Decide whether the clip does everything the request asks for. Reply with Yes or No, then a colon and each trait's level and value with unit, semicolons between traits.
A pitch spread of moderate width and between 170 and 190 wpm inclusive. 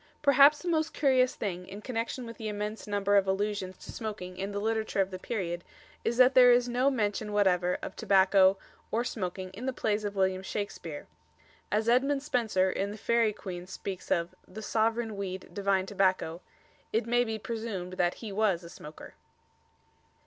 Yes: average, 3.7 semitones; average, 180 wpm